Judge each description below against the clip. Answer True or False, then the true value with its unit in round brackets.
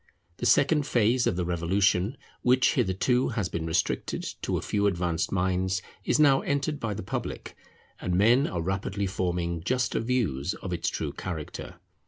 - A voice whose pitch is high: False (95 Hz)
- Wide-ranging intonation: True (5.8 semitones)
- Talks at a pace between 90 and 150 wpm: False (165 wpm)